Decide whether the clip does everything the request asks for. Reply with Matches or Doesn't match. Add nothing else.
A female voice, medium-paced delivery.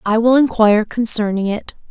Matches